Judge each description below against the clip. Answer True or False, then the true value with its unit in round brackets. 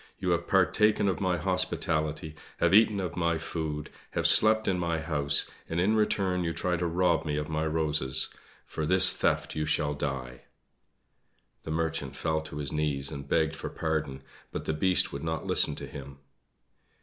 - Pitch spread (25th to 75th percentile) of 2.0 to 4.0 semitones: True (3.2 semitones)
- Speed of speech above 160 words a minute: True (180 wpm)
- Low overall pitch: True (80 Hz)